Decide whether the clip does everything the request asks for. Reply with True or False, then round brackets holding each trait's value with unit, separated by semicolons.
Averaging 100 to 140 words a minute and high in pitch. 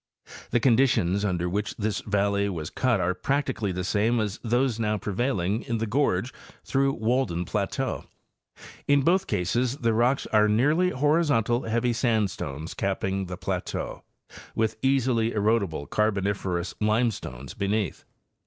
False (135 wpm; 110 Hz)